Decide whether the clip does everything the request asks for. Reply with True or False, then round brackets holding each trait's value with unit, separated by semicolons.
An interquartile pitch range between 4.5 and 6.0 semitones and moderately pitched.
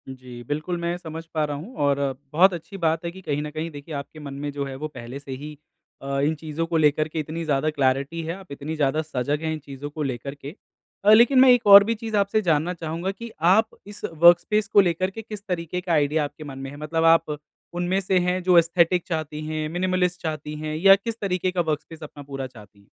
False (3.8 semitones; 160 Hz)